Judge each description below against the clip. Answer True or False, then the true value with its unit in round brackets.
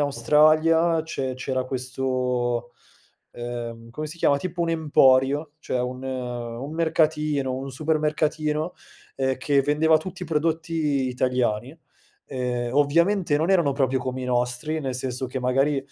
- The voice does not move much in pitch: False (3.5 semitones)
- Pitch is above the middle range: False (135 Hz)